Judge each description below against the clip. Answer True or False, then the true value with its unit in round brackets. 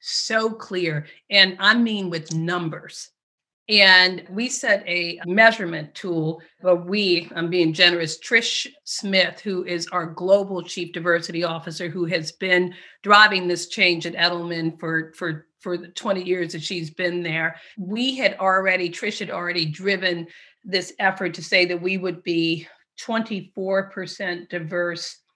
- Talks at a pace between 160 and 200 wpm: False (145 wpm)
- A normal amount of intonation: False (2.3 semitones)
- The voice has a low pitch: False (180 Hz)